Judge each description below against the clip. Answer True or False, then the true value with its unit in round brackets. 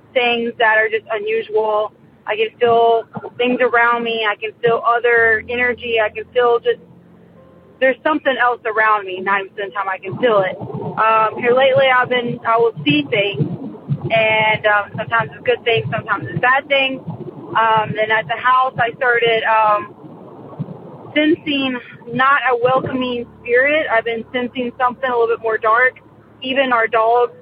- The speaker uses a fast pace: False (170 wpm)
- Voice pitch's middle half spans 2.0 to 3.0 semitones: True (2.4 semitones)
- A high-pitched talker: True (235 Hz)